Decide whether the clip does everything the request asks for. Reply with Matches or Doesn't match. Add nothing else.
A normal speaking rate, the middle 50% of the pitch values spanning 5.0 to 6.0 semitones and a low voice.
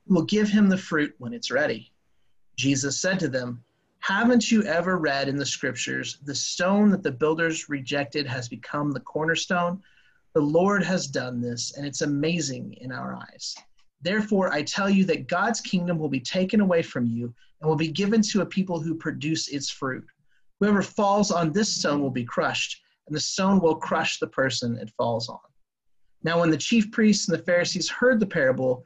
Doesn't match